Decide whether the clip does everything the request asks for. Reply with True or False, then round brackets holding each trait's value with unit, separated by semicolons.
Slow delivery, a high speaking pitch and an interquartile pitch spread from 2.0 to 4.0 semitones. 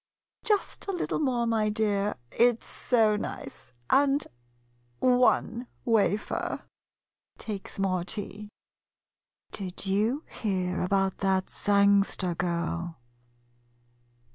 True (105 wpm; 205 Hz; 3.6 semitones)